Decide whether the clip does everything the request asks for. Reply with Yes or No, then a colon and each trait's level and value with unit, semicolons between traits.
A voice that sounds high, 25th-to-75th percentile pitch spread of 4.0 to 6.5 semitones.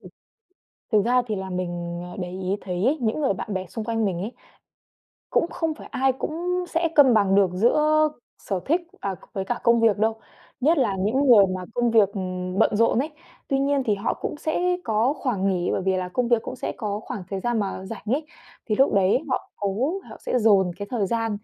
Yes: high, 220 Hz; average, 5.2 semitones